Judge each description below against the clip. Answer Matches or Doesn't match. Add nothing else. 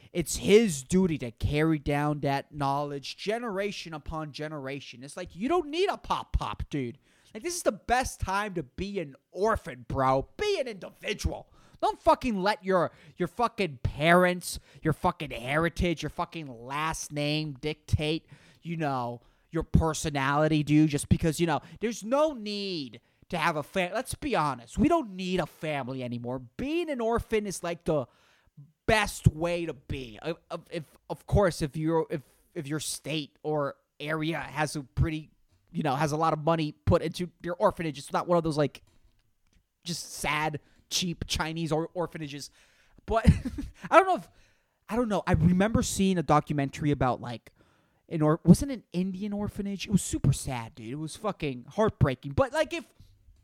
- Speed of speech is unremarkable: Matches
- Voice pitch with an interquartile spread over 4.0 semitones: Matches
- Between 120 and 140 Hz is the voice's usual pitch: Doesn't match